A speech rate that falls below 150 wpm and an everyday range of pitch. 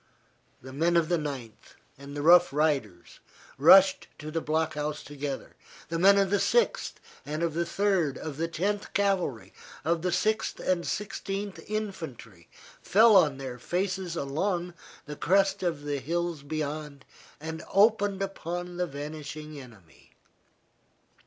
Yes: average, 140 wpm; average, 4.7 semitones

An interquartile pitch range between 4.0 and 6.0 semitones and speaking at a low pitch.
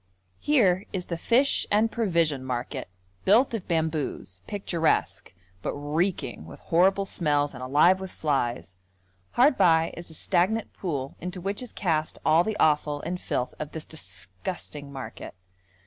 No: average, 4.8 semitones; medium, 165 Hz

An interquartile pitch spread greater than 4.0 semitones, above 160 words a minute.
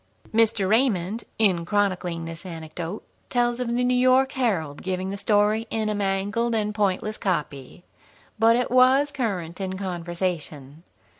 No: average, 4.7 semitones; average, 145 wpm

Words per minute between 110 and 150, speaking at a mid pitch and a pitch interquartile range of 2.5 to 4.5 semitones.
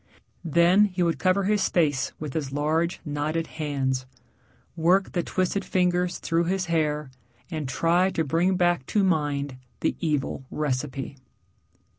Yes: average, 140 wpm; medium, 165 Hz; average, 3.5 semitones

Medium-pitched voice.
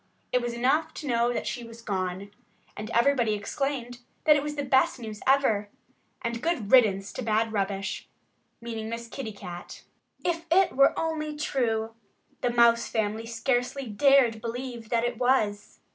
No: high, 235 Hz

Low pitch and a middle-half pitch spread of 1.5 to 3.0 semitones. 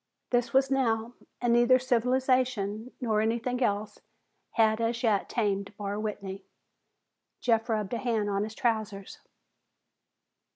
No: high, 225 Hz; average, 2.7 semitones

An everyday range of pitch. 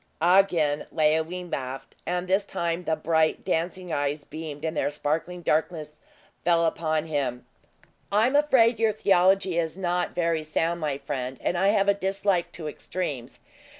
Yes: average, 3.3 semitones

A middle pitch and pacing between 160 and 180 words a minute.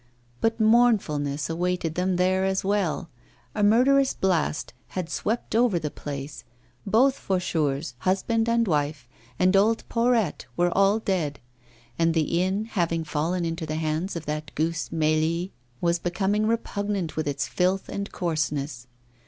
No: medium, 180 Hz; average, 145 wpm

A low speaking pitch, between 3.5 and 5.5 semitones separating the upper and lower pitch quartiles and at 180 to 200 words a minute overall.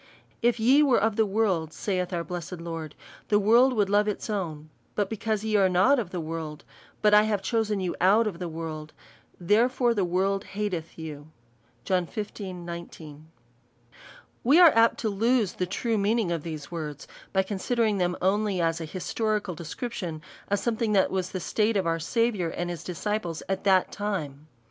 No: high, 195 Hz; average, 4.1 semitones; average, 190 wpm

